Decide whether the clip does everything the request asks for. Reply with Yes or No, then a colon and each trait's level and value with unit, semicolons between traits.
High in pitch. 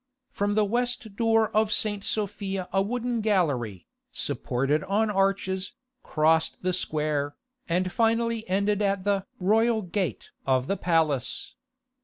Yes: high, 195 Hz